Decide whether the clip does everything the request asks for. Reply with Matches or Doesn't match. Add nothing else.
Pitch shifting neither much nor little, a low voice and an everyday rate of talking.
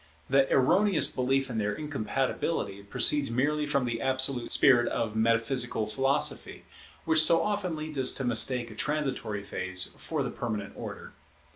Matches